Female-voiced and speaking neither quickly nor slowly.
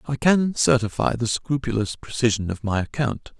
No: male; average, 160 wpm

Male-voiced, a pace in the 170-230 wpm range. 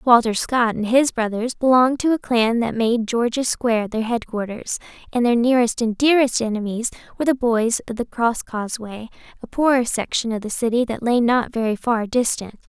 No: female; average, 185 wpm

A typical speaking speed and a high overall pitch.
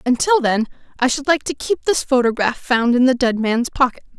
No: fast, 215 wpm; very high, 255 Hz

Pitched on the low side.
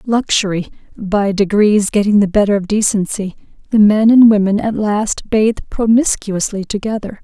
No: high, 210 Hz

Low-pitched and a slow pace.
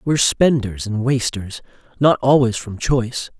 Yes: low, 120 Hz; slow, 125 wpm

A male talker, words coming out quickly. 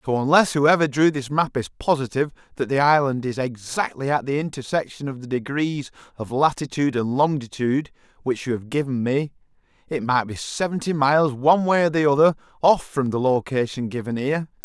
No: male; average, 180 wpm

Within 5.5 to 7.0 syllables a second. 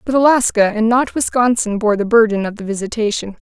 Yes: 5.8 syllables/s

